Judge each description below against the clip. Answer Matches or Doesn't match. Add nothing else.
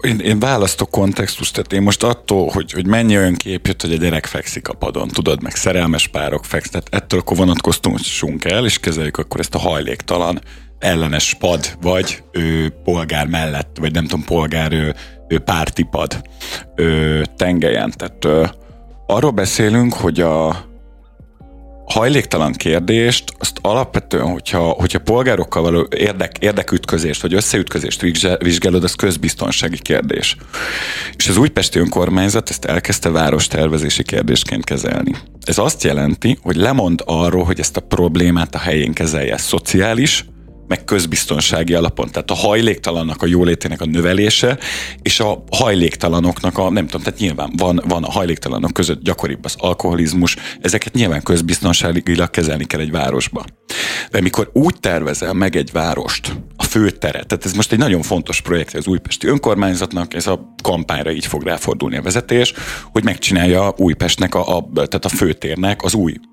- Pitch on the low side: Matches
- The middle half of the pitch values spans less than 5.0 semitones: Matches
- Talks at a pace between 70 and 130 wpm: Doesn't match